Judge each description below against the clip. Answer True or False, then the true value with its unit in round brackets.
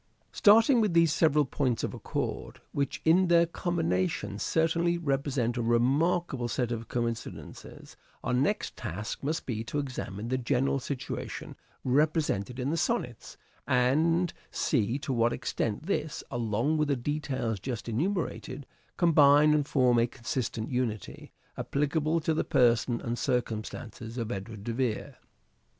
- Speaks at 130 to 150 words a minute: True (140 wpm)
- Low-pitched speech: True (130 Hz)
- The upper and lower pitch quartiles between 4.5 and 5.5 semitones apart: True (4.8 semitones)